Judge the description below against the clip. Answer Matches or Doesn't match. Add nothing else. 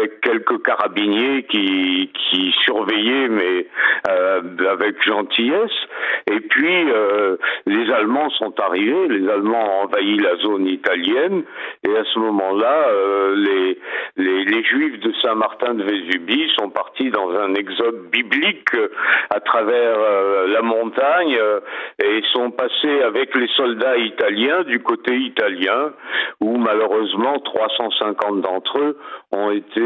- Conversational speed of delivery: Doesn't match